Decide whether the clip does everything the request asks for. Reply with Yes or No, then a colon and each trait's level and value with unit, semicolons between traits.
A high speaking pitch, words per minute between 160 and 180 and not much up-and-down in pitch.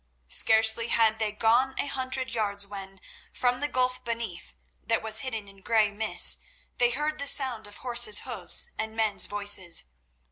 No: high, 220 Hz; average, 165 wpm; average, 3.3 semitones